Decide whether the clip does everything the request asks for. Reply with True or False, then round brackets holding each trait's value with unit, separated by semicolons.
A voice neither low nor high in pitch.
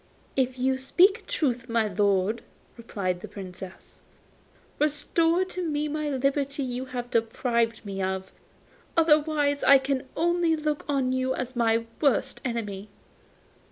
False (260 Hz)